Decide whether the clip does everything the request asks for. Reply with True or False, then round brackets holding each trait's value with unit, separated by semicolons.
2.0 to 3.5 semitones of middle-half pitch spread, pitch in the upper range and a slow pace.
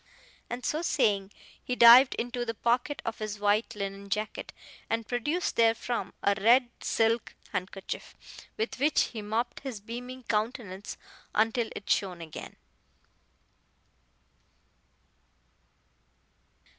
True (3.0 semitones; 230 Hz; 110 wpm)